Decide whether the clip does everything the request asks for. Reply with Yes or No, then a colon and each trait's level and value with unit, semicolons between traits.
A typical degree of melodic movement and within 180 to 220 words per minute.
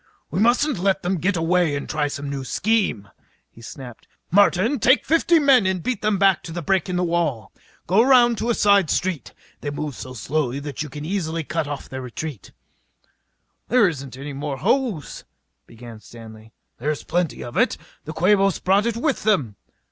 No: wide, 6.3 semitones; average, 185 wpm